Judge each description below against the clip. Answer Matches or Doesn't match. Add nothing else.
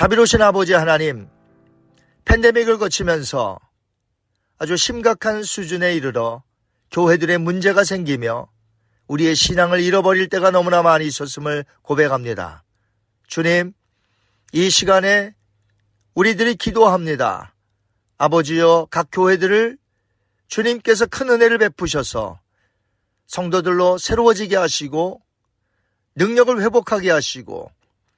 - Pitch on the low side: Doesn't match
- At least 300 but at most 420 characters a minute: Doesn't match